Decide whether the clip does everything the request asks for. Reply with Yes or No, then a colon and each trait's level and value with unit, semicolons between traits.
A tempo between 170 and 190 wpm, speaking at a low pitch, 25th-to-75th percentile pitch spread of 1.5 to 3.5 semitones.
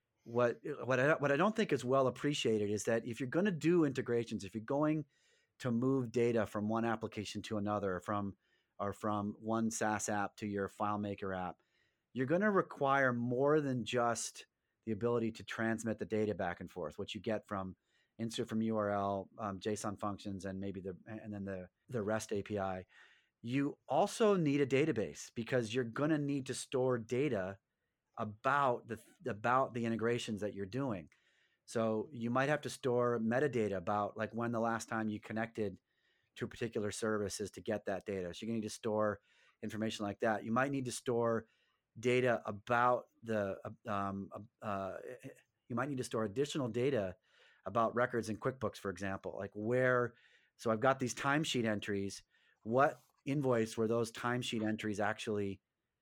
Yes: average, 180 wpm; low, 115 Hz; average, 3.2 semitones